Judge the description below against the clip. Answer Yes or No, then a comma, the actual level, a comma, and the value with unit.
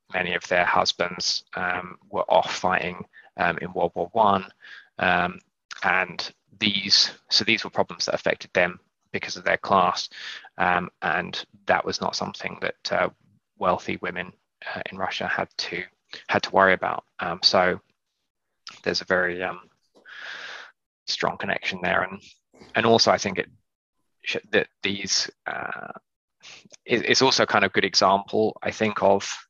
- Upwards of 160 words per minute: No, average, 155 wpm